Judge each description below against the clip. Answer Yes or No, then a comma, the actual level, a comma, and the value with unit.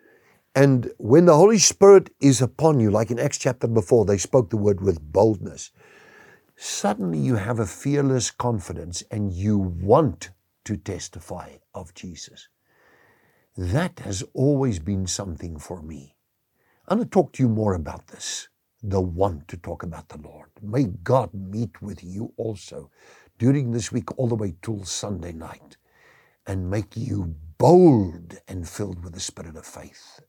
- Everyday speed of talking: Yes, average, 160 wpm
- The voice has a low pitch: Yes, low, 105 Hz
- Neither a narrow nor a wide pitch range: No, wide, 5.7 semitones